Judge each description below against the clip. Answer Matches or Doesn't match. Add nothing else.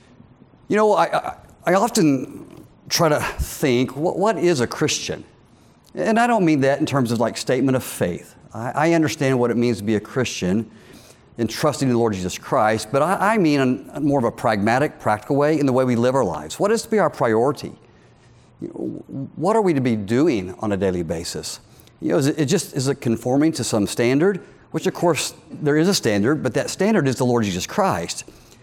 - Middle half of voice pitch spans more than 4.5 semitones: Matches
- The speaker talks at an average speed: Doesn't match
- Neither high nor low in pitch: Doesn't match